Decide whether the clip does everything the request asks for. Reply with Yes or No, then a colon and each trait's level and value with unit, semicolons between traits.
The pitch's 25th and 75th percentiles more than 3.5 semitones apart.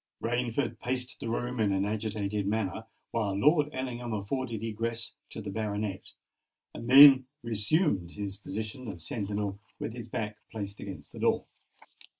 No: average, 3.1 semitones